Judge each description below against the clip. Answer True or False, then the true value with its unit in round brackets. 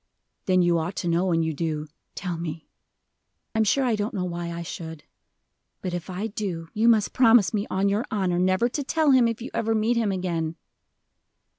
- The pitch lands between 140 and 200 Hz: True (185 Hz)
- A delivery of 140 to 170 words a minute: False (200 wpm)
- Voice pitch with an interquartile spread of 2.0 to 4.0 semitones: False (4.6 semitones)